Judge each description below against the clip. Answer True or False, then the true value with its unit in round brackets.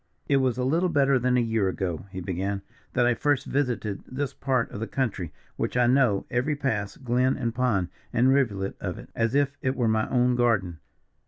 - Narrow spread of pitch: False (4.2 semitones)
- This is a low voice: True (120 Hz)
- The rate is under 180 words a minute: False (205 wpm)